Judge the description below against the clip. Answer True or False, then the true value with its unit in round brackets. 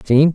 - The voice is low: False (145 Hz)